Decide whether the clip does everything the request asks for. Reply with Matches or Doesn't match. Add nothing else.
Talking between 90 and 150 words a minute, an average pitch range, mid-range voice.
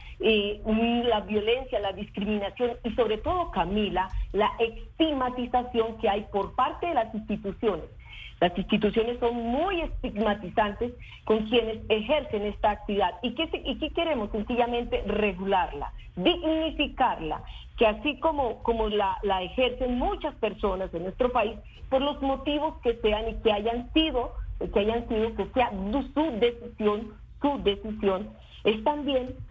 Doesn't match